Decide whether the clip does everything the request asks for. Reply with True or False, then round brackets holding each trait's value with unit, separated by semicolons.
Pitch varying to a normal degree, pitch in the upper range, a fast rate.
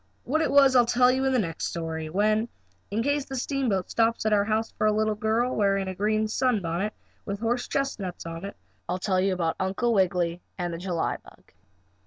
True (4.6 semitones; 215 Hz; 210 wpm)